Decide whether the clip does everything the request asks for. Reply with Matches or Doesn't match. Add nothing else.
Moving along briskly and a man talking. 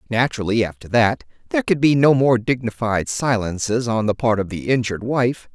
Doesn't match